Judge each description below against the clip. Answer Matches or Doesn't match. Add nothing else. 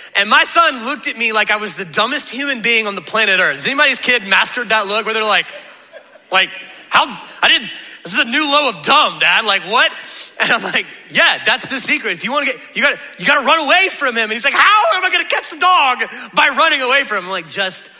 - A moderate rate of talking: Doesn't match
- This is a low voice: Doesn't match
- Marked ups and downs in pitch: Matches